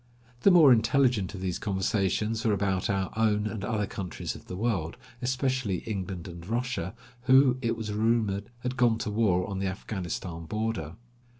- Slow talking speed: No, average, 170 wpm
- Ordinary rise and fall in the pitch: Yes, average, 3.7 semitones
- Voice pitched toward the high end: No, low, 105 Hz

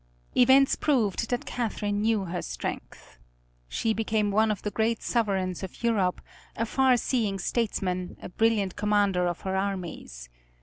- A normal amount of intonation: Yes, average, 3.3 semitones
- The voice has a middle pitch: No, high, 210 Hz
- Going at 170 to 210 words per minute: No, average, 145 wpm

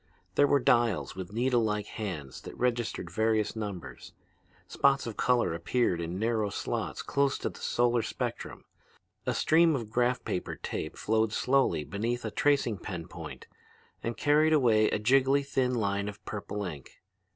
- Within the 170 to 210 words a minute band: No, average, 155 wpm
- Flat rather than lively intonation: No, average, 3.9 semitones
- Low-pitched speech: Yes, low, 110 Hz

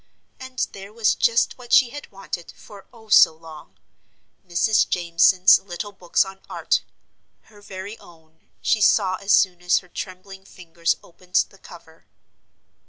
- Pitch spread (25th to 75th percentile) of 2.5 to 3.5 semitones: Yes, average, 3.0 semitones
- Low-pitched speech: No, high, 190 Hz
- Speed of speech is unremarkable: Yes, average, 150 wpm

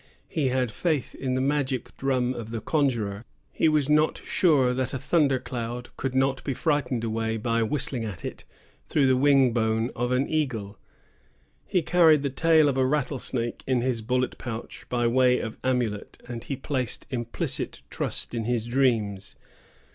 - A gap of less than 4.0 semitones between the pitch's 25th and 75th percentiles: Yes, average, 2.9 semitones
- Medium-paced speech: Yes, average, 170 wpm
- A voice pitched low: Yes, low, 125 Hz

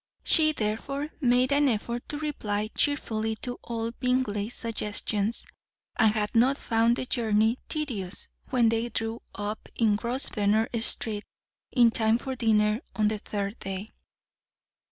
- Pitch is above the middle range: Yes, high, 225 Hz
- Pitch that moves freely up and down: No, average, 2.9 semitones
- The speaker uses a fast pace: No, slow, 135 wpm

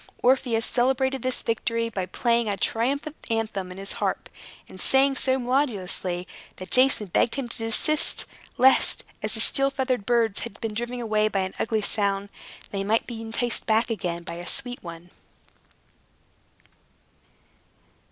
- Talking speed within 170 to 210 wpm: No, average, 150 wpm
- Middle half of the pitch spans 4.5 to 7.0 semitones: No, average, 4.1 semitones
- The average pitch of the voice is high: Yes, high, 225 Hz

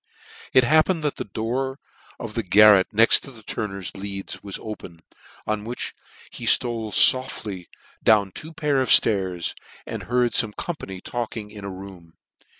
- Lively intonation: No, average, 4.1 semitones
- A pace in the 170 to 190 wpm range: No, average, 155 wpm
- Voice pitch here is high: No, low, 110 Hz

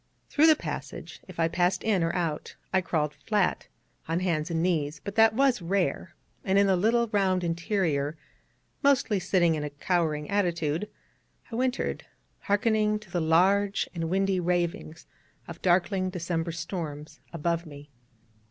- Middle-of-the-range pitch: Yes, medium, 180 Hz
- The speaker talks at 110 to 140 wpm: No, average, 150 wpm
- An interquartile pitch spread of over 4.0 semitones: No, average, 3.5 semitones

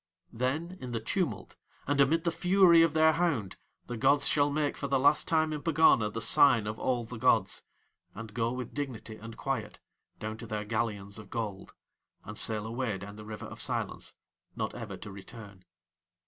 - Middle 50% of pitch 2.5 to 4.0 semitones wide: No, average, 5.3 semitones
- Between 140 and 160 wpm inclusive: No, average, 190 wpm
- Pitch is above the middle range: No, low, 120 Hz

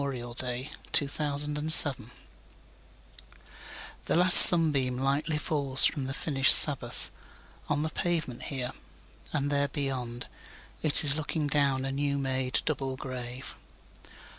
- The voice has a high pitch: No, medium, 140 Hz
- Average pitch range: No, narrow, 2.2 semitones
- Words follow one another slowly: Yes, slow, 105 wpm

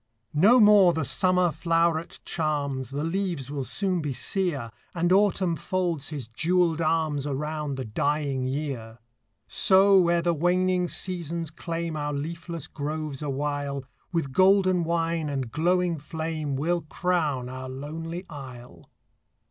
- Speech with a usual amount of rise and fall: Yes, average, 3.7 semitones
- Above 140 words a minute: No, slow, 135 wpm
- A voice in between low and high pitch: Yes, medium, 160 Hz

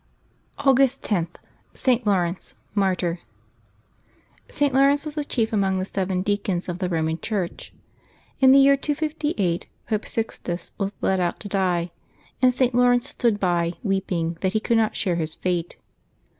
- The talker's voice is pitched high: Yes, high, 200 Hz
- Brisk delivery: No, average, 155 wpm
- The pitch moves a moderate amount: No, wide, 5.9 semitones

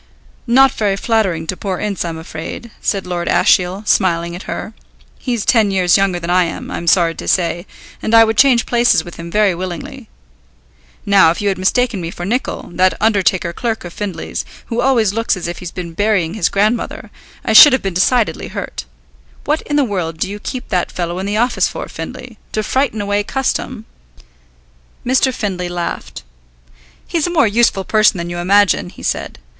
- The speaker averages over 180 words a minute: Yes, average, 190 wpm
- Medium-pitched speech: No, high, 200 Hz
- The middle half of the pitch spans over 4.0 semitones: Yes, average, 4.4 semitones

